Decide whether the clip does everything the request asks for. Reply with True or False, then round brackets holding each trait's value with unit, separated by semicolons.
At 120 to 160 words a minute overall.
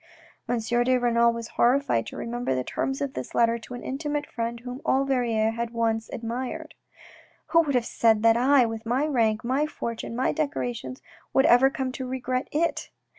False (190 wpm)